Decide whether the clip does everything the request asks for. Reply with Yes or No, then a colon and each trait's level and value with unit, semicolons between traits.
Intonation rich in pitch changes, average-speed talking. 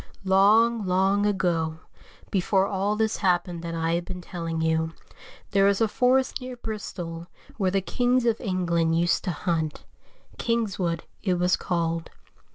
No: average, 3.7 semitones; average, 150 wpm